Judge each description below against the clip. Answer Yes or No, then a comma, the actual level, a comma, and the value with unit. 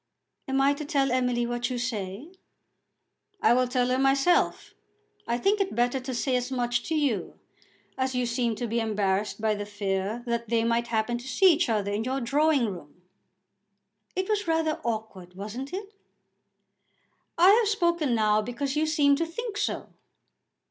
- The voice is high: Yes, high, 245 Hz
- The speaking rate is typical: Yes, average, 175 wpm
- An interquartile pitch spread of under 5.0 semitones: Yes, average, 4.6 semitones